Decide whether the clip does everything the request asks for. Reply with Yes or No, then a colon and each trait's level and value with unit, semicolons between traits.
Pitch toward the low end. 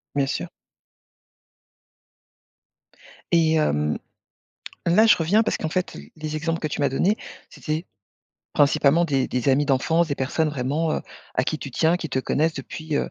No: medium, 155 Hz